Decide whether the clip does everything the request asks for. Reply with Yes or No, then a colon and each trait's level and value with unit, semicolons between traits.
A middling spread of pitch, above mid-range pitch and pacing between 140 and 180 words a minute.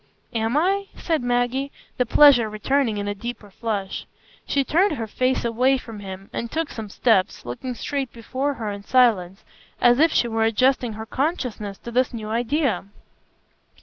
Yes: average, 3.9 semitones; high, 240 Hz; average, 170 wpm